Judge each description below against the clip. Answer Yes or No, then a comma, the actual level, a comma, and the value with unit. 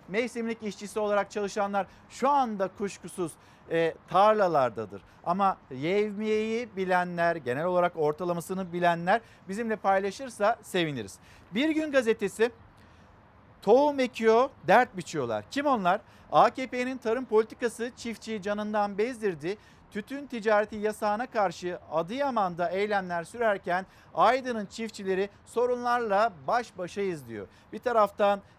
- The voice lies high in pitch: Yes, high, 200 Hz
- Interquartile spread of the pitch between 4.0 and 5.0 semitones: Yes, average, 4.5 semitones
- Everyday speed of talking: Yes, average, 105 wpm